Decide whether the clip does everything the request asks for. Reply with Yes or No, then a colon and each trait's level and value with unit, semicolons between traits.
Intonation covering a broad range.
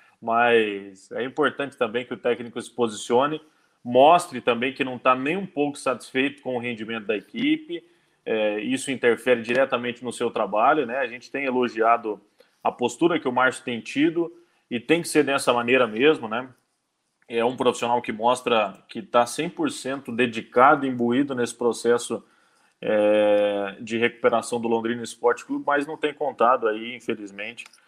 No: average, 3.1 semitones